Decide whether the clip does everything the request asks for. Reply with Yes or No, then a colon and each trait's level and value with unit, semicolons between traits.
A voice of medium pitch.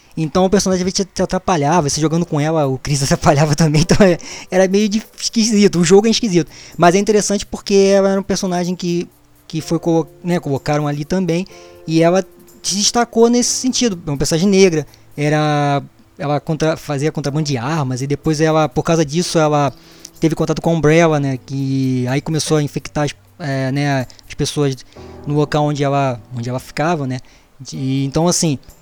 Yes: medium, 155 Hz